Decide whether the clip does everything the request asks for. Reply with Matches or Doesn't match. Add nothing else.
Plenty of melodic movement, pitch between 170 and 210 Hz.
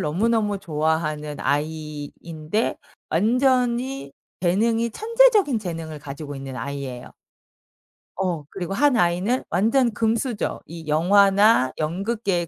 Matches